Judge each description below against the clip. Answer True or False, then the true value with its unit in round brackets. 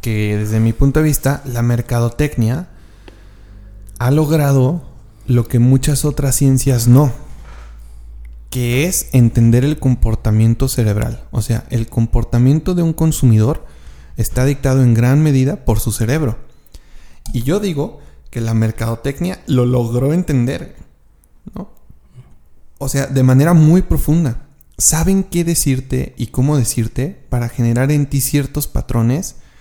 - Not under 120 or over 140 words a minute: True (130 wpm)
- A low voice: True (125 Hz)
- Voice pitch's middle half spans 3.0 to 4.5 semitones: True (3.9 semitones)